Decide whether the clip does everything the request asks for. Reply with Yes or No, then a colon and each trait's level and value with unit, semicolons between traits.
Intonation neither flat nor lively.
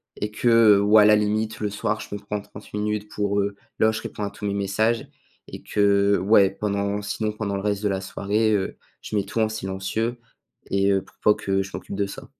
No: narrow, 1.2 semitones